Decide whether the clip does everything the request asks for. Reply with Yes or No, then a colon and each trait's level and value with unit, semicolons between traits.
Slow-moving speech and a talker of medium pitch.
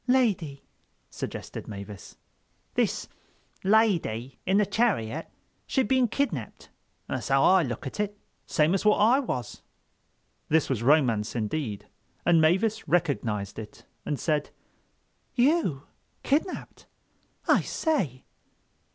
Yes: slow, 110 wpm; medium, 160 Hz